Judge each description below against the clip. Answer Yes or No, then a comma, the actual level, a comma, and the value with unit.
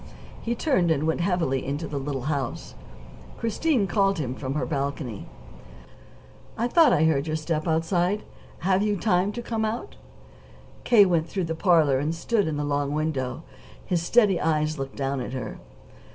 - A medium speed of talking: Yes, average, 180 wpm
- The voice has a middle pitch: Yes, medium, 160 Hz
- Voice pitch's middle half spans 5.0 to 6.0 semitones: Yes, wide, 5.5 semitones